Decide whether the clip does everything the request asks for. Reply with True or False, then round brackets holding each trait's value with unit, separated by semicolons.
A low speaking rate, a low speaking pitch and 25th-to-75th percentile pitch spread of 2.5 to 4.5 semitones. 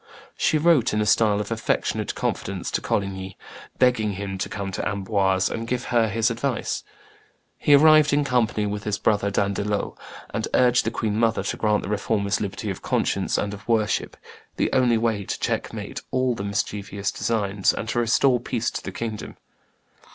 False (180 wpm; 110 Hz; 2.8 semitones)